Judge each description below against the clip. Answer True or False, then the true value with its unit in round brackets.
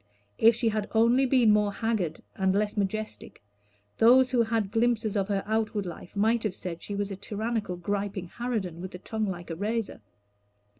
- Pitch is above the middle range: True (210 Hz)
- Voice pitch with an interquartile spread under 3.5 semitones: True (2.7 semitones)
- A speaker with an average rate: True (185 wpm)